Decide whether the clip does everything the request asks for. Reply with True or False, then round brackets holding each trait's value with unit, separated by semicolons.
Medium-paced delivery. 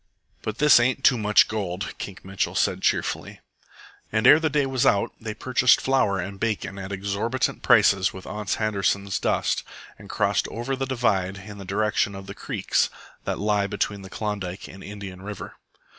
True (175 wpm)